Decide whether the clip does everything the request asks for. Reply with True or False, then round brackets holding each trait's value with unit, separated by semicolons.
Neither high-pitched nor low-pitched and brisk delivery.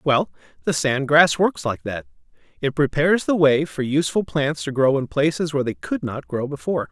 True (145 Hz; 210 wpm)